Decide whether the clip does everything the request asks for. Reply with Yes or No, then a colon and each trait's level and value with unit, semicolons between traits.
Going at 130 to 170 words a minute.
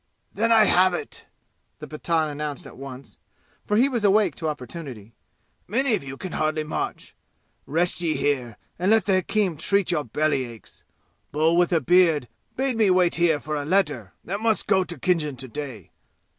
No: average, 185 wpm